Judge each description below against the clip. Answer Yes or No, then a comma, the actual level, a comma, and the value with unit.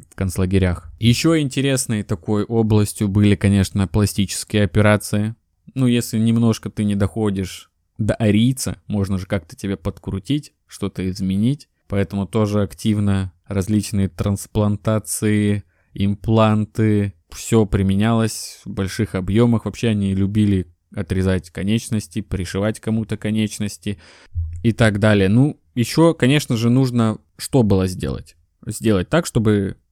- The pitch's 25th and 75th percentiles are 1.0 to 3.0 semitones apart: Yes, narrow, 2.5 semitones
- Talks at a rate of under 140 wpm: Yes, average, 115 wpm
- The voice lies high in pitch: No, low, 105 Hz